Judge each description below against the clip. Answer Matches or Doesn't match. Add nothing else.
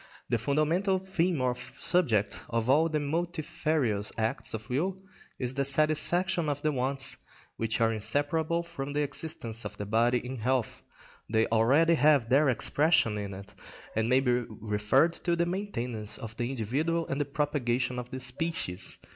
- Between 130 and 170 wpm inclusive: Matches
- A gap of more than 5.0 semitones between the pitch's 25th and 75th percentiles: Matches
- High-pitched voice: Doesn't match